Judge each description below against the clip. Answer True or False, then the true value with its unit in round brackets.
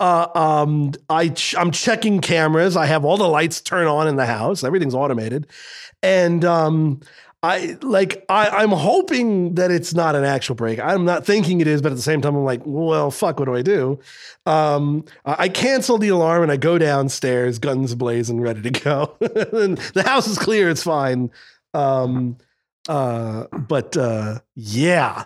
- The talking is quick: False (180 wpm)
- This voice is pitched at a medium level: True (155 Hz)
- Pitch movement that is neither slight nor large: True (4.8 semitones)